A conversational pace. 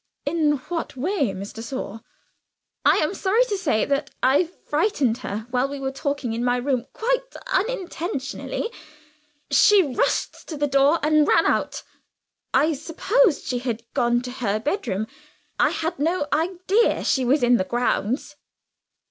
Yes: average, 150 wpm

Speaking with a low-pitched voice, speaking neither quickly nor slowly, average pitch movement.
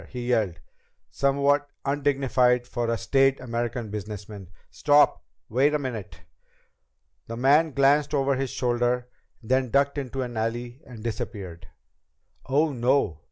No: low, 125 Hz; slow, 130 wpm; average, 3.2 semitones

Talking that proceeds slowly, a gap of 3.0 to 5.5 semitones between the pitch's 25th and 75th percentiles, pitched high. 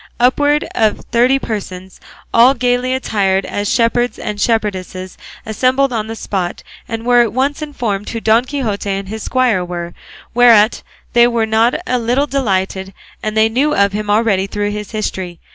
No: average, 165 wpm; average, 3.6 semitones; high, 220 Hz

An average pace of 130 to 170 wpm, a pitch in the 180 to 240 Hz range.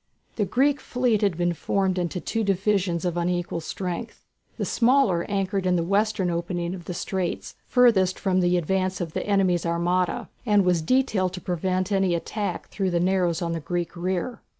No: average, 180 wpm; medium, 185 Hz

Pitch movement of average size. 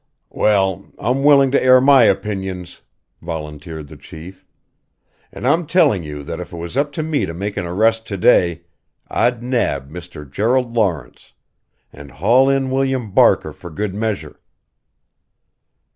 No: wide, 7.0 semitones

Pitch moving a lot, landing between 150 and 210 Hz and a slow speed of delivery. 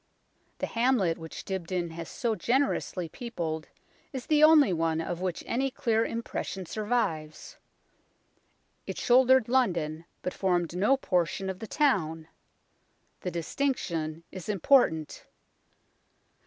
Yes: wide, 6.8 semitones; medium, 185 Hz; slow, 115 wpm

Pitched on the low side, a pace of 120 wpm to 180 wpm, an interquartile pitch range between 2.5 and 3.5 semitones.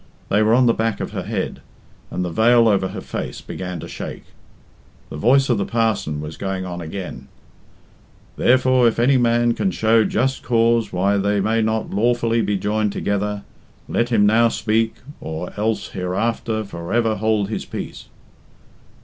Yes: low, 110 Hz; average, 170 wpm; average, 2.8 semitones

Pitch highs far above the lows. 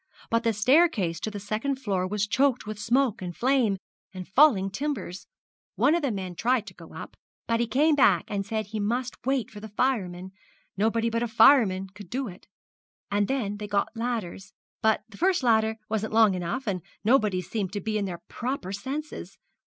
No: average, 4.4 semitones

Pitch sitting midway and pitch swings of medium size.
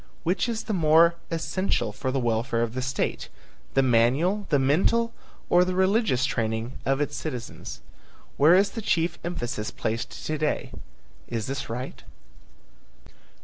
No: medium, 145 Hz; wide, 6.5 semitones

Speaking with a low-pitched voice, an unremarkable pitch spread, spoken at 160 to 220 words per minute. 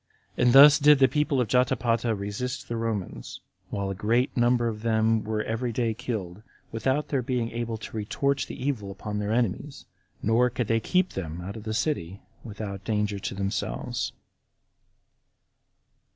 Yes: low, 115 Hz; average, 3.2 semitones; average, 165 wpm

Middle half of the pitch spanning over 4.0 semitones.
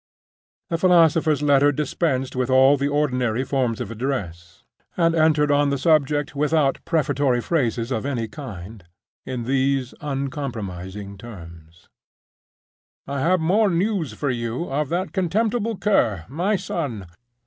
Yes: average, 5.3 semitones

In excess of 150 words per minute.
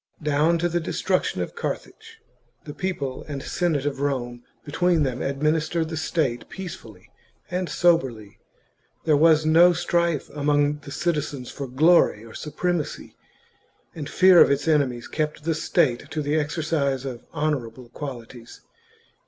No: average, 140 wpm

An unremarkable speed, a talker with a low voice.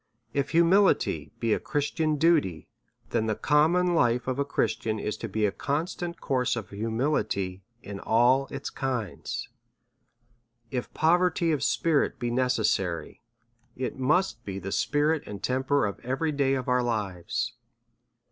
Yes: average, 150 wpm; low, 130 Hz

